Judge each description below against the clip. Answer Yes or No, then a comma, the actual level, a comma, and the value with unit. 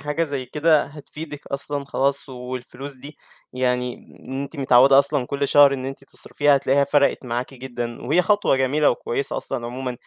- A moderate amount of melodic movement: No, narrow, 2.1 semitones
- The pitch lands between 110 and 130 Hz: No, medium, 140 Hz